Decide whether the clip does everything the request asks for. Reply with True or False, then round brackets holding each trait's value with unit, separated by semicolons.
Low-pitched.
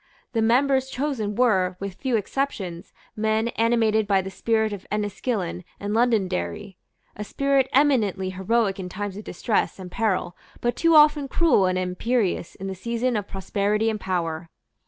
False (210 Hz)